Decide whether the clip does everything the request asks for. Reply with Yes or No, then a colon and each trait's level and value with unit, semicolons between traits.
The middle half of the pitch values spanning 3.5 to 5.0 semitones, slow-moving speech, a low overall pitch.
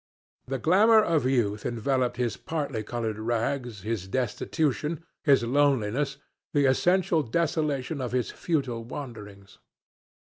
Yes: average, 4.3 semitones; slow, 110 wpm; low, 130 Hz